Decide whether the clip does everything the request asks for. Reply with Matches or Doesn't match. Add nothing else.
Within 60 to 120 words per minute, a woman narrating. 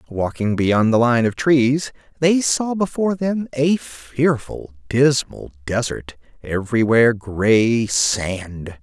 Doesn't match